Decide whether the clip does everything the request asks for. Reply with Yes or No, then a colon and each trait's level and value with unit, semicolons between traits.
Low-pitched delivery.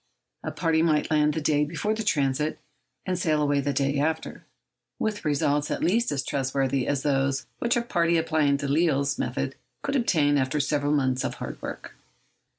No: medium, 150 Hz